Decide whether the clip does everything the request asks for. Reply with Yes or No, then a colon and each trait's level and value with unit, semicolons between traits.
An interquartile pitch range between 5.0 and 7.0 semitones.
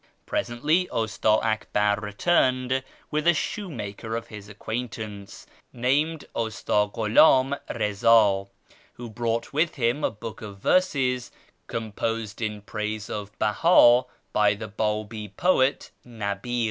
No: average, 3.4 semitones